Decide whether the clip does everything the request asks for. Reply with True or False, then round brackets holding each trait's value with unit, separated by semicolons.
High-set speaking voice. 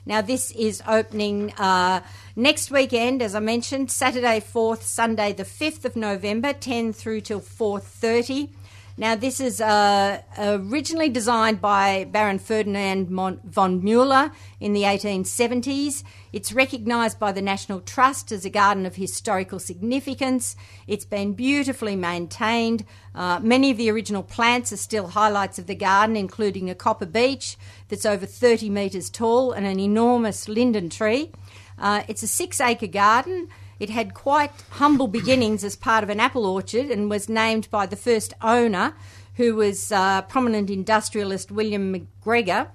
True (215 Hz)